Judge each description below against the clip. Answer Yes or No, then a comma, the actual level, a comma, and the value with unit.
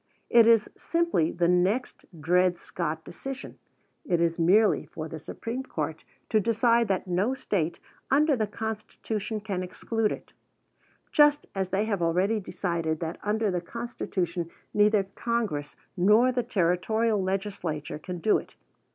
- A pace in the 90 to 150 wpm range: Yes, average, 145 wpm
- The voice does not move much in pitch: No, average, 4.5 semitones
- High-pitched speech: Yes, high, 200 Hz